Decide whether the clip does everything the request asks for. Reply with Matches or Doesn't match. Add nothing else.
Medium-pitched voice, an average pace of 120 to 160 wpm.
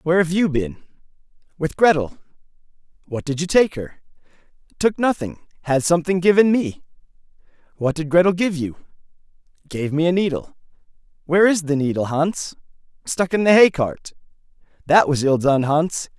Matches